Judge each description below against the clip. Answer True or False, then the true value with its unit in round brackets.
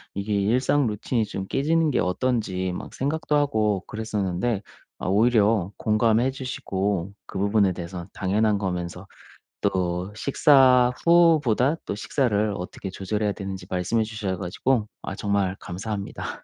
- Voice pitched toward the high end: False (105 Hz)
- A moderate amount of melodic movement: True (4.5 semitones)